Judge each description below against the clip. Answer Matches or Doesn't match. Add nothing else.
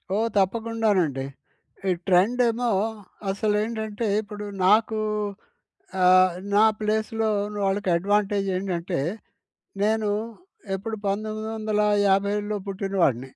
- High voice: Matches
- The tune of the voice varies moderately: Doesn't match